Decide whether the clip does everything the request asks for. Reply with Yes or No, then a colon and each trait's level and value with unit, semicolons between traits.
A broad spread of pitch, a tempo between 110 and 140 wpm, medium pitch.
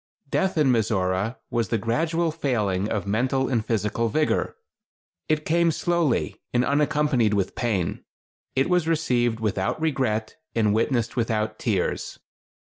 No: wide, 5.8 semitones; slow, 135 wpm; low, 120 Hz